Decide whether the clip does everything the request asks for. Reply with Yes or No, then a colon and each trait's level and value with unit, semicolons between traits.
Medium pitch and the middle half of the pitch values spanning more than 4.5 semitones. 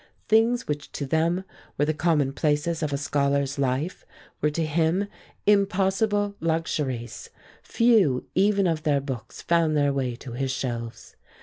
Yes: medium, 155 Hz; average, 5.1 semitones